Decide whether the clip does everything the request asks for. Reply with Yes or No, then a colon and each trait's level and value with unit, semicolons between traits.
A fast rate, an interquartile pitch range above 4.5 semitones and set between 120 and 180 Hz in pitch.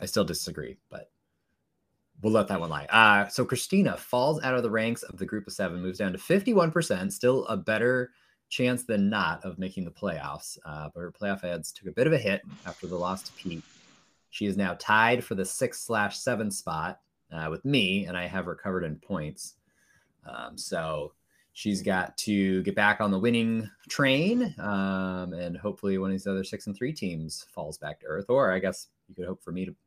No: fast, 215 wpm; average, 5.2 semitones; low, 100 Hz